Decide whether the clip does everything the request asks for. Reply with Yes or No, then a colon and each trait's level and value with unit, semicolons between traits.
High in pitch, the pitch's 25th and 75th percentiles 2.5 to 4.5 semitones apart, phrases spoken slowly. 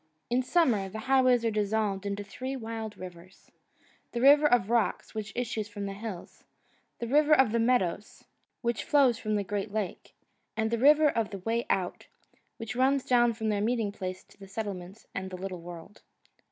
No: high, 220 Hz; average, 3.6 semitones; average, 180 wpm